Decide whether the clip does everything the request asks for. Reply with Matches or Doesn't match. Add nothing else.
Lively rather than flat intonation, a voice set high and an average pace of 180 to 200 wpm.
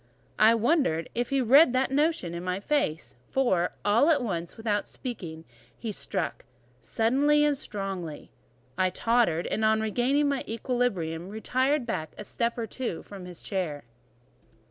Doesn't match